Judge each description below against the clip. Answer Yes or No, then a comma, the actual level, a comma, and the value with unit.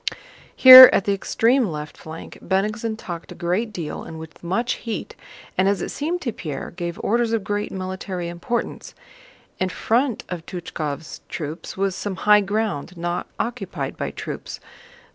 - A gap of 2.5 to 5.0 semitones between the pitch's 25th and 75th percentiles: Yes, average, 4.6 semitones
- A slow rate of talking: No, average, 160 wpm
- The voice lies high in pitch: Yes, high, 195 Hz